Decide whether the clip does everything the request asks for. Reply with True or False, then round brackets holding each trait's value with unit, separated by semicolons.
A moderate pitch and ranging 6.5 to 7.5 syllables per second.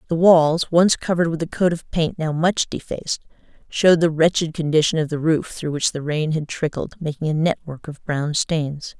False (160 Hz; 5.1 syllables/s)